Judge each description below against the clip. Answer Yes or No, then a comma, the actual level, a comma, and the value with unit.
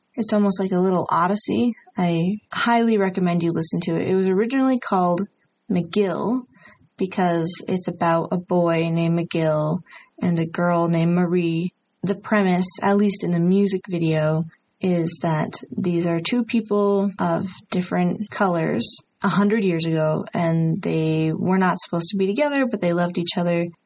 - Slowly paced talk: No, average, 160 wpm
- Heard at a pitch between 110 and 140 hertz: No, medium, 180 Hz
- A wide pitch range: No, average, 3.0 semitones